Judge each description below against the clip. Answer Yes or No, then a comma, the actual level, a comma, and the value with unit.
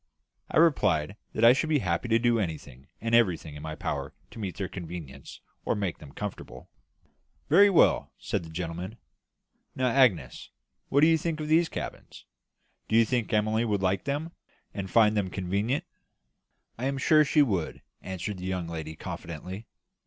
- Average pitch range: No, wide, 6.3 semitones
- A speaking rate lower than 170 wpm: No, average, 175 wpm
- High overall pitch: No, low, 105 Hz